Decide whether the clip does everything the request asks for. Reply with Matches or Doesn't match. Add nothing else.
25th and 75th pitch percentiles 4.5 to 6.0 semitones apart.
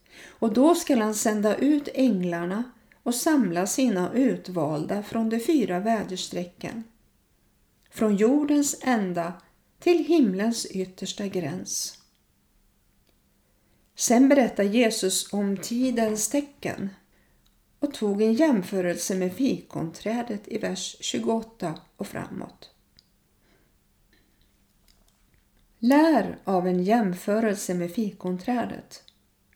Matches